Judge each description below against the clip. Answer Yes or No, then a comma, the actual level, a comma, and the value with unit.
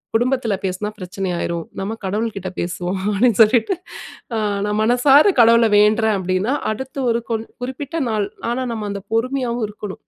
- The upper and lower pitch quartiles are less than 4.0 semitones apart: Yes, average, 3.5 semitones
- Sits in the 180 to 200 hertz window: No, high, 220 Hz